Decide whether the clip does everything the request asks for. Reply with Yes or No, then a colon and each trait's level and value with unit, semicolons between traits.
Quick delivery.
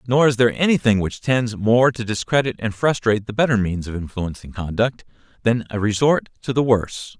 No: average, 190 wpm